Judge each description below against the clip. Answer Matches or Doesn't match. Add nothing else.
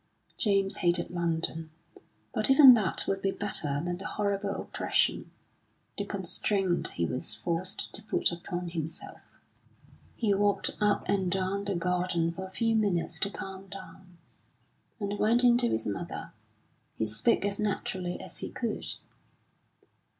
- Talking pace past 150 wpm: Doesn't match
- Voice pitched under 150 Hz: Doesn't match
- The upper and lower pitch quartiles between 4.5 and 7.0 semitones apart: Doesn't match